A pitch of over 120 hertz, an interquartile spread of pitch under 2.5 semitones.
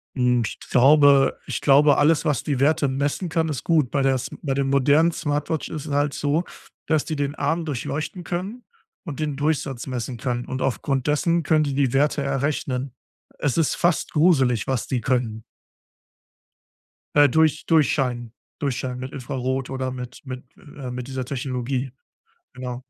No: medium, 140 Hz; average, 2.8 semitones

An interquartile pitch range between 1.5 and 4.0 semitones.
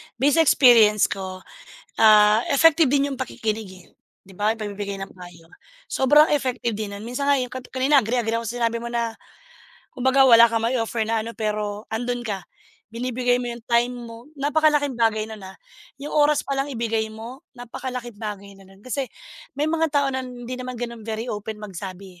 Yes: average, 3.4 semitones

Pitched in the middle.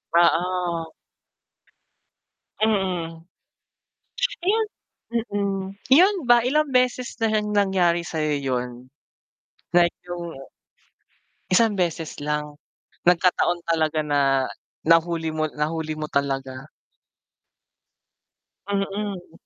Yes: medium, 175 Hz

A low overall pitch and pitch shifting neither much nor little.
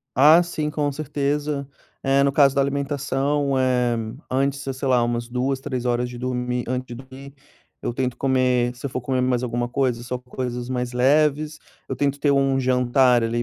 No: low, 130 Hz; narrow, 2.1 semitones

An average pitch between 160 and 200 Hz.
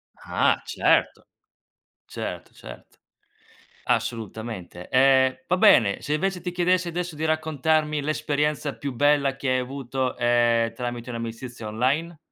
No: low, 135 Hz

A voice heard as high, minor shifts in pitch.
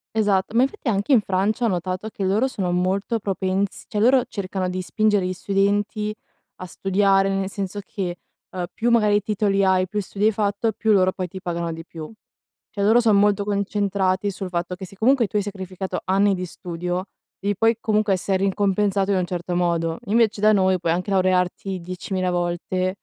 Yes: high, 195 Hz; narrow, 2.1 semitones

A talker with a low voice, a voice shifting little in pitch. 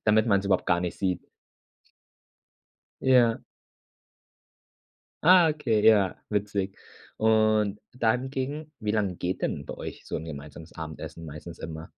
No: low, 105 Hz; average, 4.5 semitones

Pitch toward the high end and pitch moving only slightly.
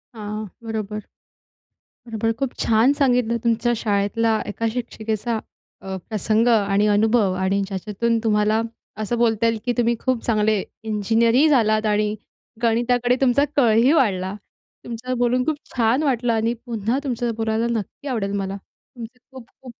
Yes: high, 225 Hz; narrow, 2.2 semitones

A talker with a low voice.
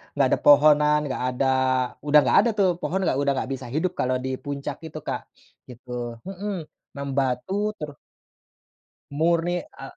No: medium, 145 Hz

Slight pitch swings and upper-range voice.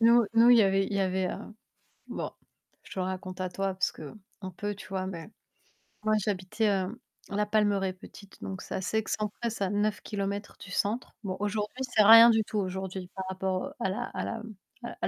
Yes: narrow, 2.3 semitones; high, 200 Hz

